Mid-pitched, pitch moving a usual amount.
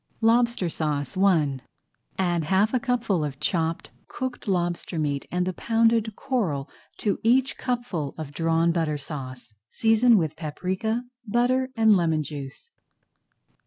No: medium, 180 Hz; wide, 6.7 semitones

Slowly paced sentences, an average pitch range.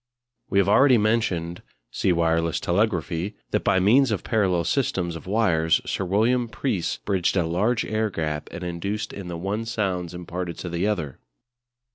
No: average, 165 wpm; average, 4.1 semitones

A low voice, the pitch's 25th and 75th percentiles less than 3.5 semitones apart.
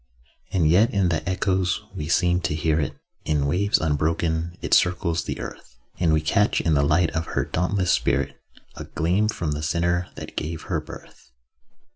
Yes: very low, 85 Hz; narrow, 2.6 semitones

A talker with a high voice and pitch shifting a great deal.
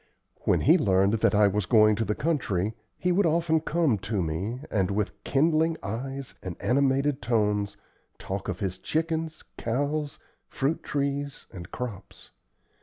No: low, 120 Hz; wide, 6.6 semitones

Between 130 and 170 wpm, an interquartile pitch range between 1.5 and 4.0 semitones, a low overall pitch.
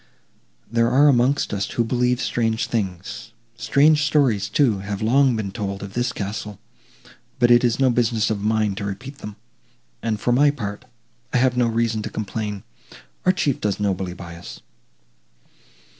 Yes: average, 165 wpm; average, 3.4 semitones; low, 115 Hz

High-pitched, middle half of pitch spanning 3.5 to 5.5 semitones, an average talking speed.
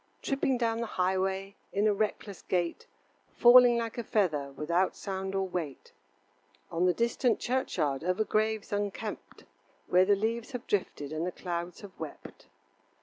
Yes: high, 195 Hz; average, 4.0 semitones; average, 150 wpm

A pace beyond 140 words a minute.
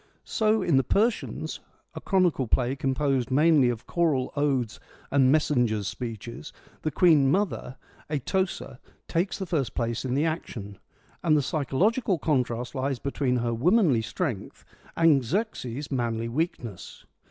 No: slow, 135 wpm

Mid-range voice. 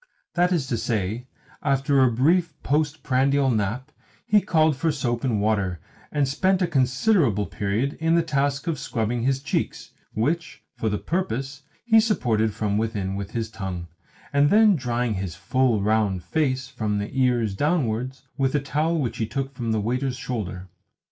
No: low, 130 Hz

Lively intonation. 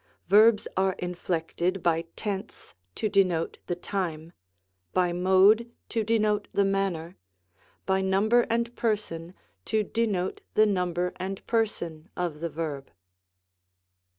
No: average, 3.5 semitones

